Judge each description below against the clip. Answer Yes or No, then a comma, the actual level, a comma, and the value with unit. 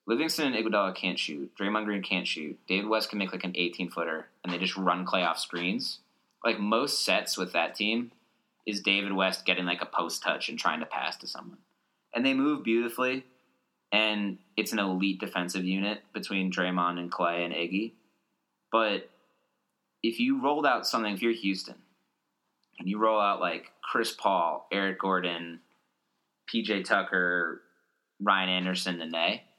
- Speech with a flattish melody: No, average, 3.4 semitones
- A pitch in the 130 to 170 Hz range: No, very low, 95 Hz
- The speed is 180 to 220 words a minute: No, average, 170 wpm